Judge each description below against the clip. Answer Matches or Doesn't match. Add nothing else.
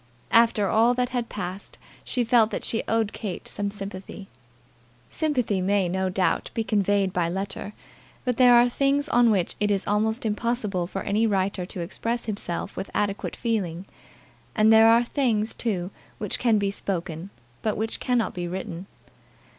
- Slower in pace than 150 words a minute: Doesn't match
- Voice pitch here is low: Doesn't match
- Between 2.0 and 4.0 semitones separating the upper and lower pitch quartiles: Matches